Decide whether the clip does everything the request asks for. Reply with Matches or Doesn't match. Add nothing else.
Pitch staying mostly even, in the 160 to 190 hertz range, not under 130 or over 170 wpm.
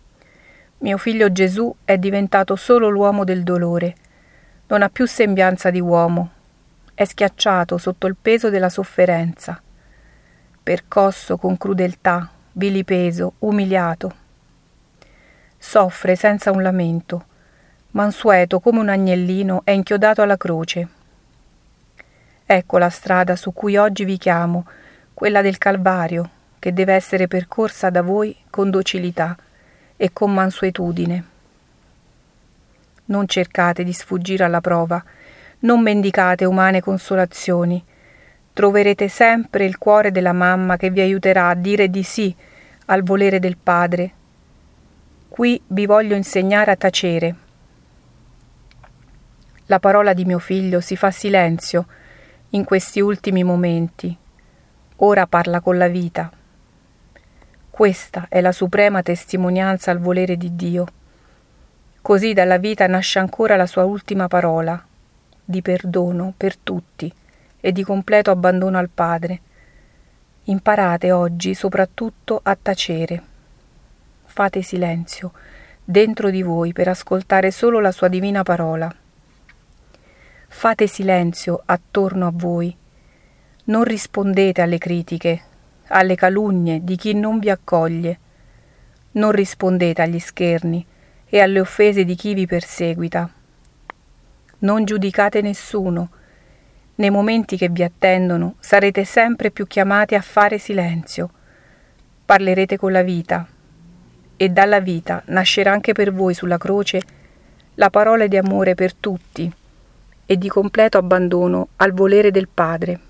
Doesn't match